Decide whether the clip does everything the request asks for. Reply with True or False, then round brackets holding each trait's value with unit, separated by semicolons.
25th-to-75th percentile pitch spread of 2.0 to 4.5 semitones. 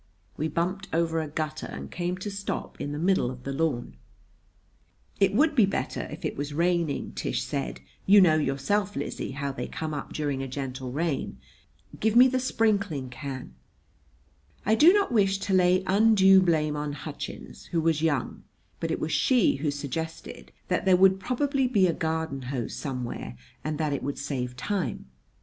False (5.5 semitones)